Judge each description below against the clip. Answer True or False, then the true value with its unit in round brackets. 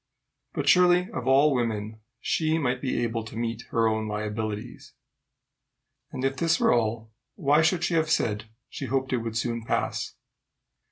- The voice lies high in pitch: False (120 Hz)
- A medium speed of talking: True (165 wpm)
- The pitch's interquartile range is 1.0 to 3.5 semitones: False (4.9 semitones)